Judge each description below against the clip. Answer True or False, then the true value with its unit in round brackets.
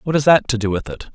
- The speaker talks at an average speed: False (365 wpm)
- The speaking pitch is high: False (125 Hz)